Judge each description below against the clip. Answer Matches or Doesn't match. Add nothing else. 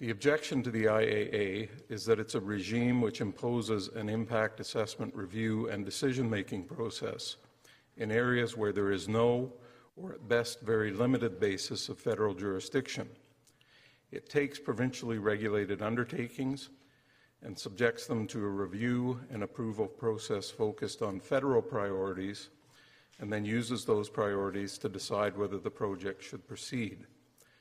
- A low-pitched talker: Matches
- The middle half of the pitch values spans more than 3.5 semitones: Doesn't match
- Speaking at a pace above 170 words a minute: Doesn't match